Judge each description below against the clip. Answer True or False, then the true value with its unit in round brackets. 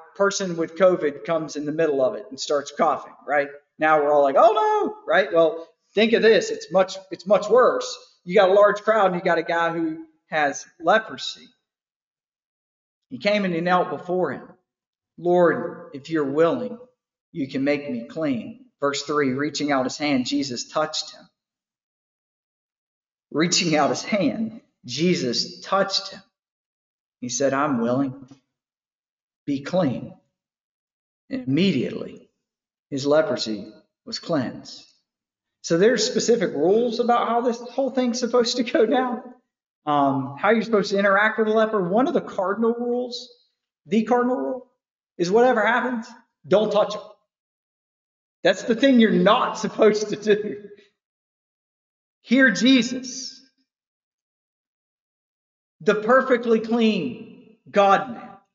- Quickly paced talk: False (140 wpm)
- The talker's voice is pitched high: True (205 Hz)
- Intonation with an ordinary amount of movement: False (7.1 semitones)